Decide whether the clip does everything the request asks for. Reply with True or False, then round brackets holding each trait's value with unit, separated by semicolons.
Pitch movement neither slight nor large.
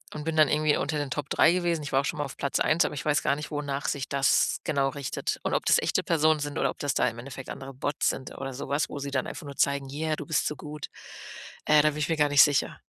False (1.6 semitones)